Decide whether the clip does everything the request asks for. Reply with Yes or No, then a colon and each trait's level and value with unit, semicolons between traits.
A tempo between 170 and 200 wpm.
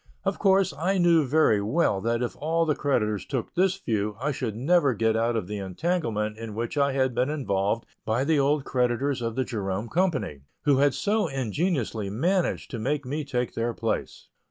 Yes: average, 195 wpm